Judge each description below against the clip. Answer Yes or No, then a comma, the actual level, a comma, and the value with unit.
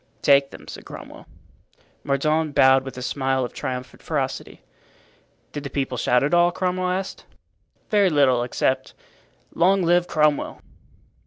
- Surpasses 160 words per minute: No, average, 140 wpm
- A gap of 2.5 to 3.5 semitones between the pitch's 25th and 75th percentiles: No, average, 4.7 semitones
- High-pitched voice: No, medium, 145 Hz